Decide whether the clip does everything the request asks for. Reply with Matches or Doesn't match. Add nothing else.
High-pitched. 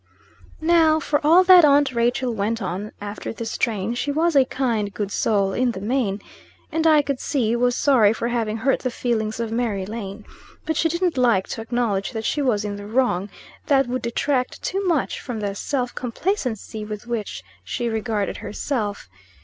Matches